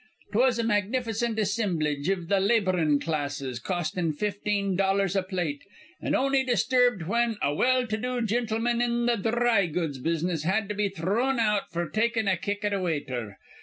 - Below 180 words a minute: Yes, average, 170 wpm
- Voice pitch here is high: Yes, high, 200 Hz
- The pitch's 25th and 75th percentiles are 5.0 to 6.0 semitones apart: Yes, average, 5.3 semitones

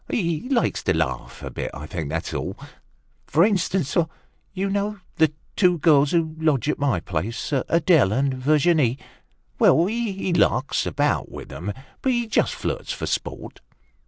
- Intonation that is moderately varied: No, wide, 6.6 semitones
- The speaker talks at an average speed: Yes, average, 160 wpm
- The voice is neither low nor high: Yes, medium, 155 Hz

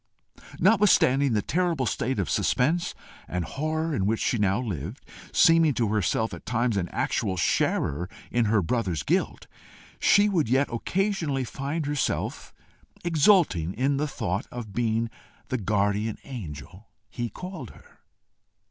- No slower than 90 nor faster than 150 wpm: Yes, average, 140 wpm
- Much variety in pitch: Yes, wide, 6.9 semitones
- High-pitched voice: No, low, 120 Hz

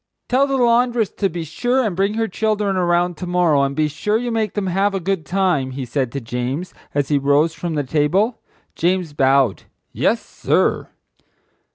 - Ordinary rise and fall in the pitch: No, wide, 6.3 semitones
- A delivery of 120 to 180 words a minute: No, average, 190 wpm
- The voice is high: No, medium, 175 Hz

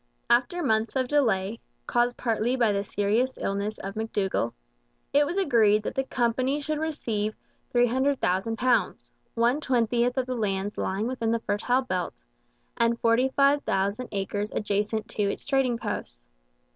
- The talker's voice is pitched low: No, high, 230 Hz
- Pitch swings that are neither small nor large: Yes, average, 3.8 semitones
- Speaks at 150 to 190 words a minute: No, average, 140 wpm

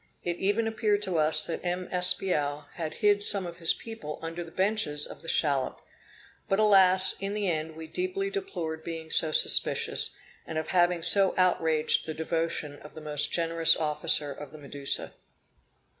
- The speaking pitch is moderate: Yes, medium, 170 Hz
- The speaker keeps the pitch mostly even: No, average, 3.7 semitones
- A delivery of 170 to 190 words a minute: Yes, average, 175 wpm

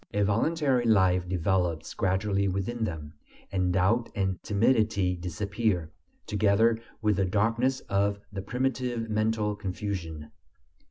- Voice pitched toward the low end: Yes, low, 100 Hz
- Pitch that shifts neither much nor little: Yes, average, 3.3 semitones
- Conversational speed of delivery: No, slow, 115 wpm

